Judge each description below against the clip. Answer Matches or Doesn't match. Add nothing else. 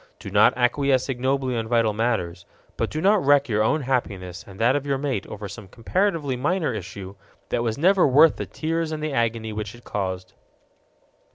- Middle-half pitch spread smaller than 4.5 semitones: Doesn't match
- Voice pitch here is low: Matches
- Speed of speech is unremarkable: Matches